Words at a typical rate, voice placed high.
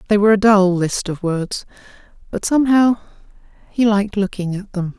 Yes: average, 170 wpm; high, 200 Hz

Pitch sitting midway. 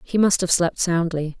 Yes: medium, 170 Hz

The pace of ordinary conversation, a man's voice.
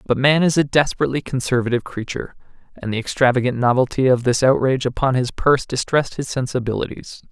Yes: average, 165 wpm; male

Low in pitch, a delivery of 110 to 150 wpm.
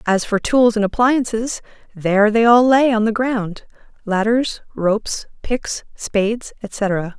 No: high, 220 Hz; slow, 135 wpm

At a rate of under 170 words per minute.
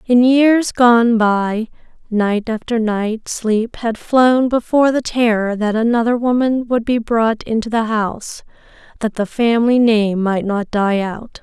Yes: average, 160 wpm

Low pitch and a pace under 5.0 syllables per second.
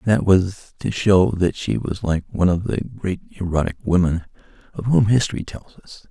Yes: very low, 95 Hz; 4.7 syllables/s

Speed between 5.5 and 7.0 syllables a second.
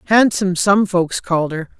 No: 5.2 syllables/s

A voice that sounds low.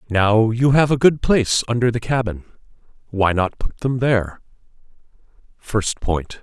Yes: low, 115 Hz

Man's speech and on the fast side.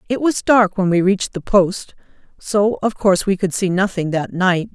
No: female; fast, 215 wpm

